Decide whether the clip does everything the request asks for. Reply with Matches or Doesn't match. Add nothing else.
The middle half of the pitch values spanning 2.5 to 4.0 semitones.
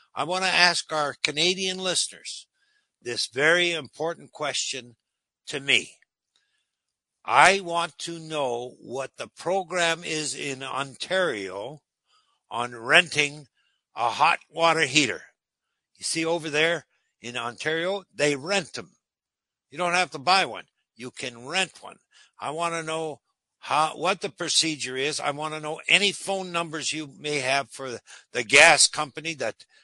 Matches